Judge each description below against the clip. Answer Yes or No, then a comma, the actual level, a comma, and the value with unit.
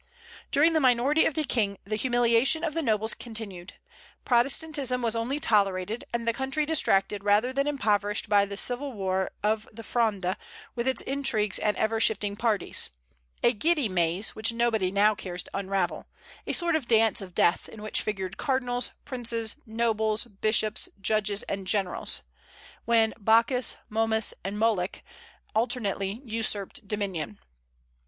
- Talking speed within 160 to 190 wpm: No, average, 150 wpm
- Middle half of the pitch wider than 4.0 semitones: No, average, 3.3 semitones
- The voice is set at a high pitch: Yes, high, 220 Hz